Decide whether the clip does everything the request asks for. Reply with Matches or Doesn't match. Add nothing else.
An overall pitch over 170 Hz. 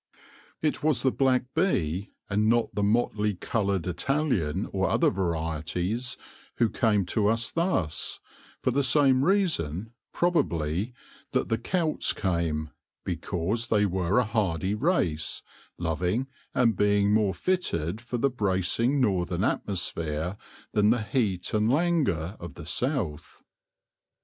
Doesn't match